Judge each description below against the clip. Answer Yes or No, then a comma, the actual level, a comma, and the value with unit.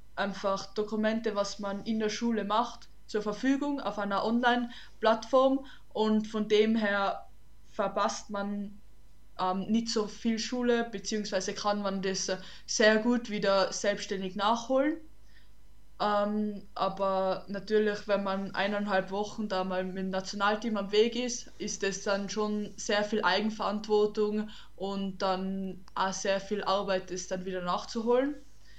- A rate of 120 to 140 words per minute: Yes, average, 135 wpm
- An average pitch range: No, narrow, 1.9 semitones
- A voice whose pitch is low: No, high, 205 Hz